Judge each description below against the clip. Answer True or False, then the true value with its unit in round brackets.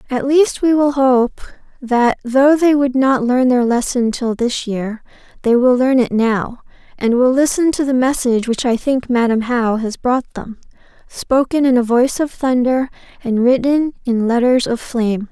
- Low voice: False (250 Hz)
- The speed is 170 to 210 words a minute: True (185 wpm)